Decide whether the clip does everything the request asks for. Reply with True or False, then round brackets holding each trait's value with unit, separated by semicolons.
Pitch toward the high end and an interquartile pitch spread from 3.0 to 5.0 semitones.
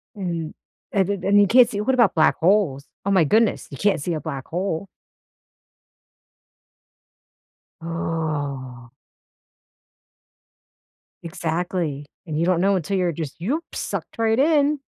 False (180 Hz; 4.3 semitones)